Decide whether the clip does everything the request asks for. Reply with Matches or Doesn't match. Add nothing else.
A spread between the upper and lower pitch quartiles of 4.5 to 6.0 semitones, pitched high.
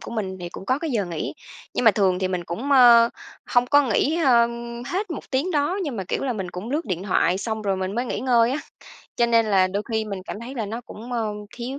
Matches